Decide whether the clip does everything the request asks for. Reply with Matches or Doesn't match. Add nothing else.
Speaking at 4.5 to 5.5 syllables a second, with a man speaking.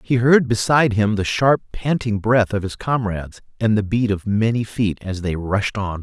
Matches